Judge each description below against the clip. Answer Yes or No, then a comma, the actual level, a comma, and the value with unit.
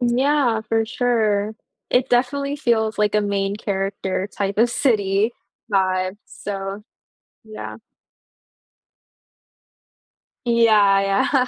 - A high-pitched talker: Yes, high, 215 Hz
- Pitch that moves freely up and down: No, average, 3.5 semitones